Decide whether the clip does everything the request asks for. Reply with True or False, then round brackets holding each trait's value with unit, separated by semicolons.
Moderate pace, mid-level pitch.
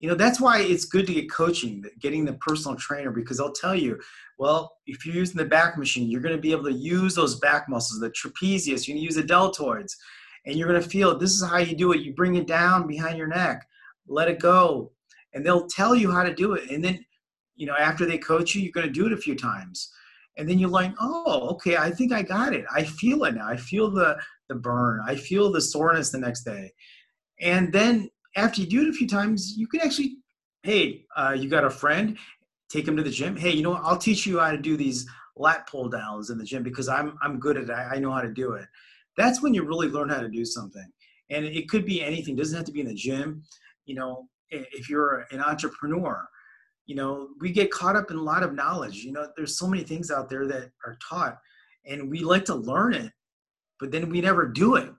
False (250 wpm; 160 Hz)